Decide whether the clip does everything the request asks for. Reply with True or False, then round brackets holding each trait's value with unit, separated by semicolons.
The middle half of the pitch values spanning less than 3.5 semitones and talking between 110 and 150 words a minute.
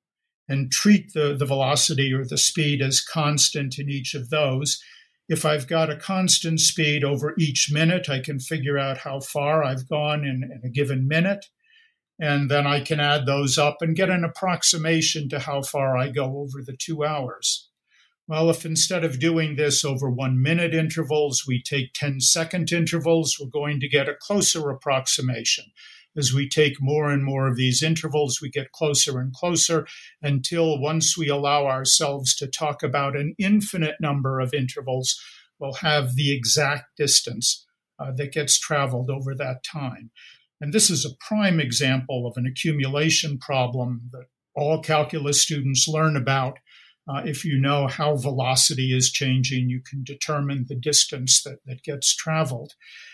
False (2.7 semitones; 170 wpm)